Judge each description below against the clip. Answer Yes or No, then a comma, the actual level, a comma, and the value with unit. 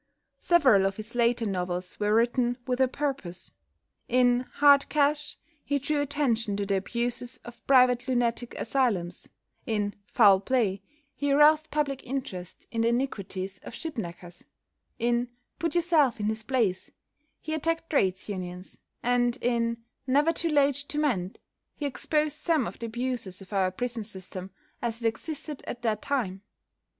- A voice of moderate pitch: No, high, 240 Hz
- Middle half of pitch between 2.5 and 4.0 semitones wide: No, wide, 5.5 semitones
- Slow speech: No, average, 155 wpm